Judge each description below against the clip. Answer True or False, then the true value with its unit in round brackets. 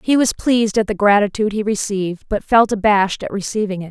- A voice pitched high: True (210 Hz)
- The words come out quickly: True (215 wpm)